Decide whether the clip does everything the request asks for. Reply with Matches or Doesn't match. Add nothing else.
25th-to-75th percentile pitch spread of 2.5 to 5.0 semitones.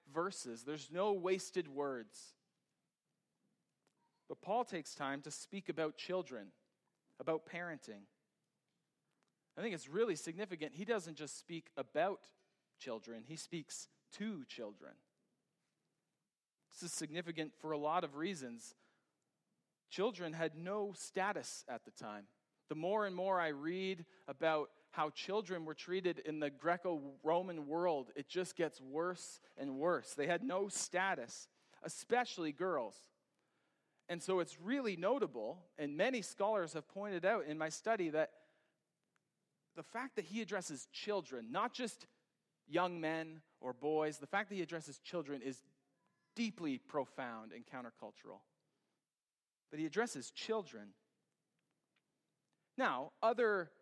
Matches